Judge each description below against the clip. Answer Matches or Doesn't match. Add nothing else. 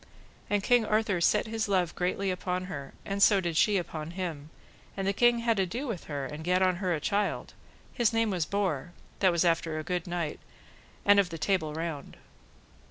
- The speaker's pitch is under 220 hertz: Matches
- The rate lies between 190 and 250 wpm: Matches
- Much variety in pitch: Doesn't match